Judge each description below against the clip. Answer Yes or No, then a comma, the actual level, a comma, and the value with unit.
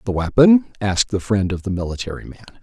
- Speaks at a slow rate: No, fast, 205 wpm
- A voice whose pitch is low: Yes, low, 105 Hz